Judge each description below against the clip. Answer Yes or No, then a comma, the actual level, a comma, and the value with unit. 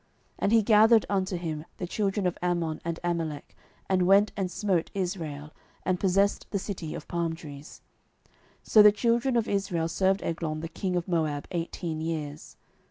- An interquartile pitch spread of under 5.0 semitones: Yes, average, 3.4 semitones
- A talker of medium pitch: Yes, medium, 175 Hz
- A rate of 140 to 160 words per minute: No, average, 175 wpm